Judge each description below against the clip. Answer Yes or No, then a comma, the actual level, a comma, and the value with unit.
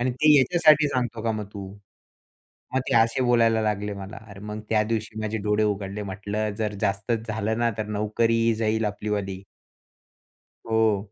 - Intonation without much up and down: Yes, narrow, 1.8 semitones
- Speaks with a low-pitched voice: Yes, low, 110 Hz